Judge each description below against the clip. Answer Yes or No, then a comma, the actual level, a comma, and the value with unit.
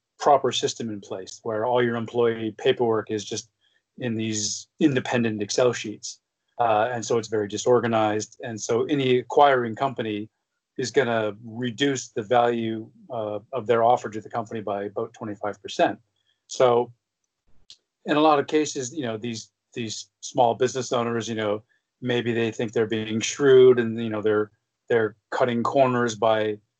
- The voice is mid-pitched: No, low, 115 Hz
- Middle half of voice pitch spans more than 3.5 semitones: No, narrow, 2.4 semitones